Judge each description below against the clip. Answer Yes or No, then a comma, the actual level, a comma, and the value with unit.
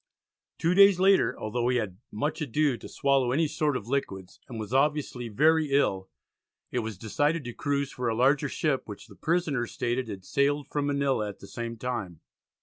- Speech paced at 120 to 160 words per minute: No, average, 190 wpm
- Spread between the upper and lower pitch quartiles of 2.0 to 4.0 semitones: No, average, 4.7 semitones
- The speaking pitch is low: Yes, low, 130 Hz